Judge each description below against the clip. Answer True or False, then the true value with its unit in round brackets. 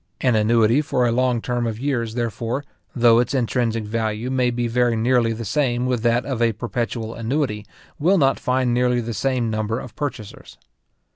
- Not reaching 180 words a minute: False (185 wpm)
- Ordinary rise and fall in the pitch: False (1.9 semitones)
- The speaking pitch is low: True (120 Hz)